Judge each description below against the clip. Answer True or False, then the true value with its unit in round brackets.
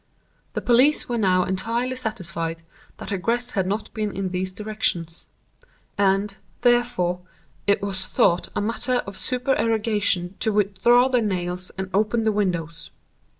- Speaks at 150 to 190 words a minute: False (140 wpm)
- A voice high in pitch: True (205 Hz)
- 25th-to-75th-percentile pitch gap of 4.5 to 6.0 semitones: False (4.0 semitones)